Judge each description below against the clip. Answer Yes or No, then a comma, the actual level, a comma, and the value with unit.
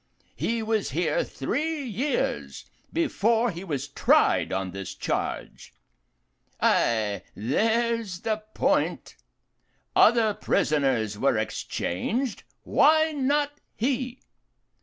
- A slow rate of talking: Yes, slow, 95 wpm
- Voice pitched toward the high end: Yes, high, 220 Hz